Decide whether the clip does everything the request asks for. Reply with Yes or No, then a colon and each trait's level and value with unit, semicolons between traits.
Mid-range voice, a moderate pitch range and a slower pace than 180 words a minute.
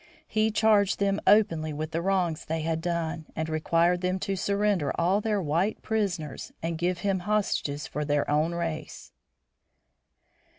Yes: medium, 170 Hz; average, 4.0 semitones; average, 155 wpm